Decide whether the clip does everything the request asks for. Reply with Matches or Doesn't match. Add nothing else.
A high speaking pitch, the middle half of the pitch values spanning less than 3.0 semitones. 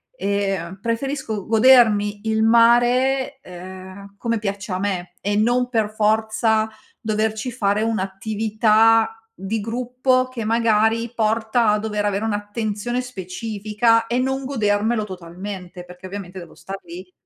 Matches